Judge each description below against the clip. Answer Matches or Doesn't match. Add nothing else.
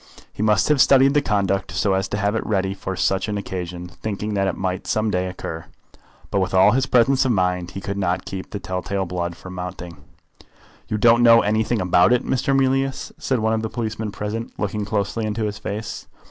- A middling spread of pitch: Matches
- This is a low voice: Matches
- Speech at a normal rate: Doesn't match